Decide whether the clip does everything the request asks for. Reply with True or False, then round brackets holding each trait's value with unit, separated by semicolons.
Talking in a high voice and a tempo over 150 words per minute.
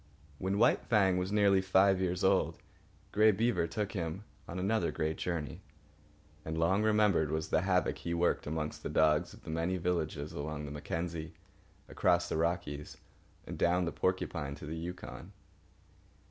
False (85 Hz; 160 wpm)